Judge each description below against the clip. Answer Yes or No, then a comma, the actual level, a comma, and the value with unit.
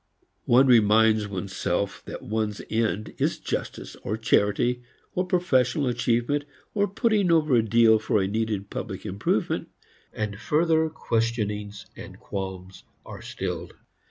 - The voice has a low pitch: Yes, low, 110 Hz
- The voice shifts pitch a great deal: No, average, 4.3 semitones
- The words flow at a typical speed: No, slow, 130 wpm